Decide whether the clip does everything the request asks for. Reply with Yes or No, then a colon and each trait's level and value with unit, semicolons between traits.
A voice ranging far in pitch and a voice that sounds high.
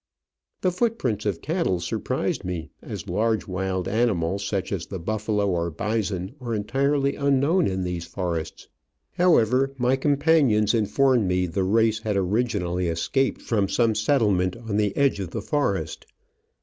No: wide, 5.7 semitones; low, 105 Hz